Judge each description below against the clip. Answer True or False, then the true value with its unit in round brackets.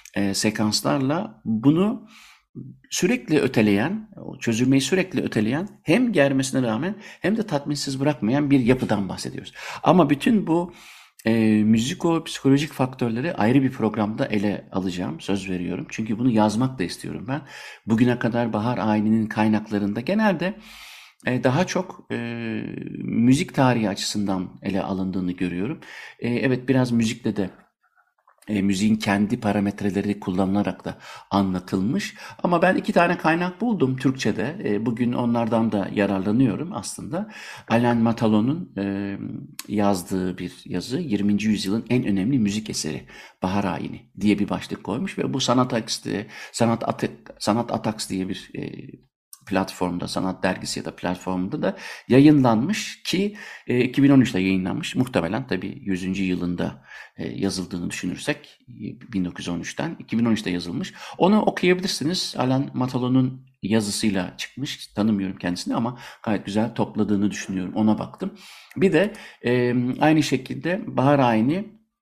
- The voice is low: True (110 Hz)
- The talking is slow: False (125 wpm)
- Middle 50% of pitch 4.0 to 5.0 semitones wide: False (5.4 semitones)